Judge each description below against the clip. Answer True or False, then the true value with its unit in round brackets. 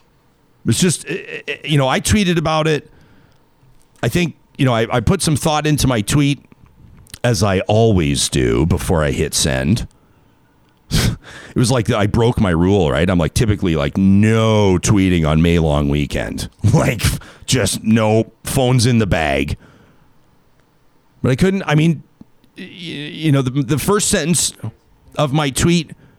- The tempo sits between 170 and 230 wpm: False (155 wpm)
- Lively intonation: True (6.7 semitones)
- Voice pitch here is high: False (125 Hz)